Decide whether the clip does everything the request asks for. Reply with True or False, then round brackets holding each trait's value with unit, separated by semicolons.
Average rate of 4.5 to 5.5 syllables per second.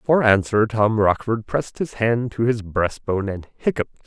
True (4.9 syllables/s)